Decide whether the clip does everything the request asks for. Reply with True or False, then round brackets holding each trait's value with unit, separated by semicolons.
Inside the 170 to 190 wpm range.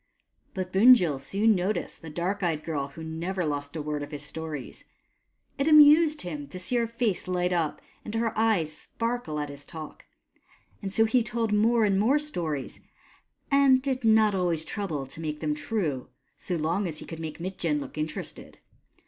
True (180 wpm)